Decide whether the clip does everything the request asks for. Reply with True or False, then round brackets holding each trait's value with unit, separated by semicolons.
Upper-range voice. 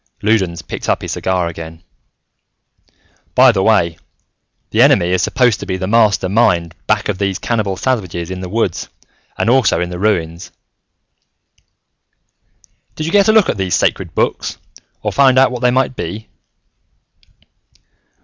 False (100 Hz)